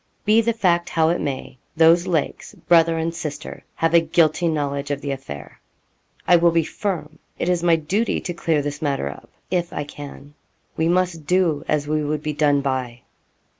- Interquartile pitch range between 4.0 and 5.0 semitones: No, average, 2.9 semitones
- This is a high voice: No, medium, 160 Hz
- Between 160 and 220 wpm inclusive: Yes, average, 190 wpm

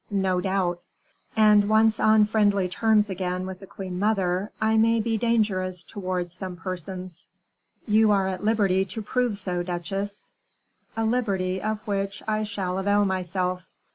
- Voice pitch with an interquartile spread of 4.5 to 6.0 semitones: No, narrow, 2.6 semitones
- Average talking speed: Yes, average, 150 wpm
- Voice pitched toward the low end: No, high, 195 Hz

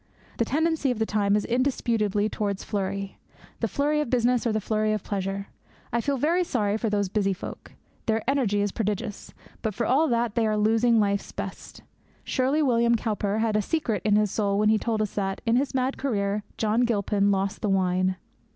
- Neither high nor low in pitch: No, high, 215 Hz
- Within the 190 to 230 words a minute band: Yes, average, 200 wpm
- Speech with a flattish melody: No, average, 3.0 semitones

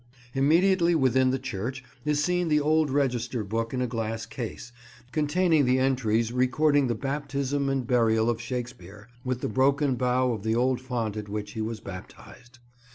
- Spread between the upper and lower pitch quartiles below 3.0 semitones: No, average, 3.6 semitones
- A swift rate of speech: No, average, 170 wpm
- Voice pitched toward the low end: Yes, low, 125 Hz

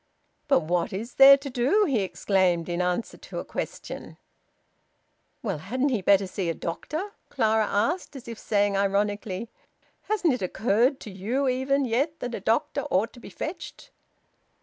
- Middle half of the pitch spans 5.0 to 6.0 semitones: Yes, wide, 5.6 semitones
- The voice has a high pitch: Yes, high, 225 Hz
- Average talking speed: Yes, average, 165 wpm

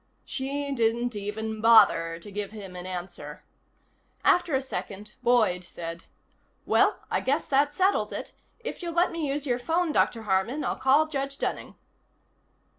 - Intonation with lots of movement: Yes, wide, 6.2 semitones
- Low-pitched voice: No, high, 240 Hz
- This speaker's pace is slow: No, average, 155 wpm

